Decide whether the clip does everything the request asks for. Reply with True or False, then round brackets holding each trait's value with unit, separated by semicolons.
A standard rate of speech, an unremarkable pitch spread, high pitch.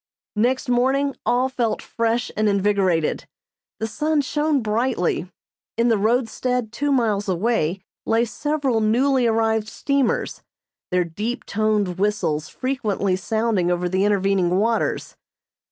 False (120 wpm; 4.0 semitones; 225 Hz)